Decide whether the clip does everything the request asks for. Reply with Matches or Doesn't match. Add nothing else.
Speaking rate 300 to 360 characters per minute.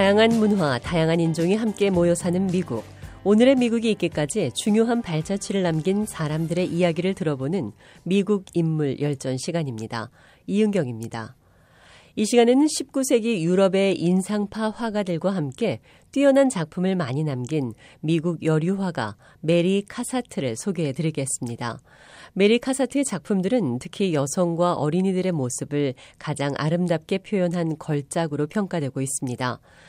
Matches